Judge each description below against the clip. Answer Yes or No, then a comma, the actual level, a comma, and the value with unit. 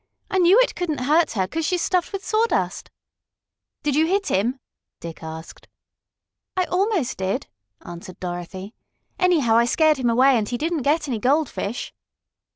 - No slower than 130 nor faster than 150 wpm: No, average, 160 wpm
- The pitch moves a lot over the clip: Yes, wide, 8.7 semitones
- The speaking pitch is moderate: No, very high, 280 Hz